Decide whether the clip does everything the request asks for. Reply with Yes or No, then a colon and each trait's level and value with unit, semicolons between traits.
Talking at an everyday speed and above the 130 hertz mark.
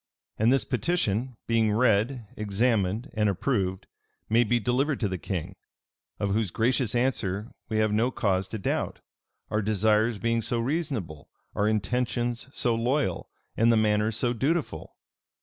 No: average, 150 wpm; low, 110 Hz